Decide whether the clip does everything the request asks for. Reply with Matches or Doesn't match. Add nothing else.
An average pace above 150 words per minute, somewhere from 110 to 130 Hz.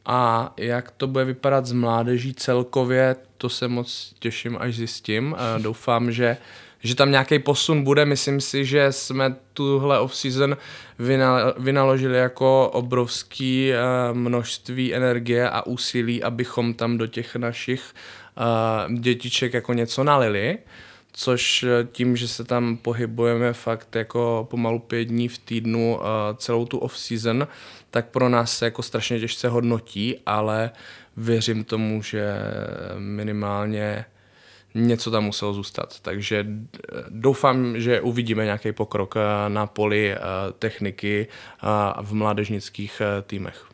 Doesn't match